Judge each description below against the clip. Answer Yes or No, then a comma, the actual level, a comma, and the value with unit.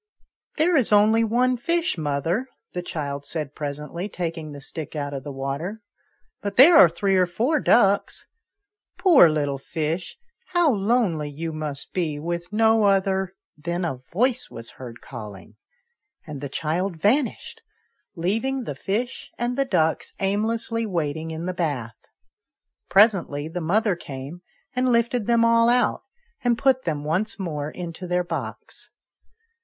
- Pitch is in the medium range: Yes, medium, 180 Hz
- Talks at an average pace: Yes, average, 155 wpm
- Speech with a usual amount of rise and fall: No, wide, 6.9 semitones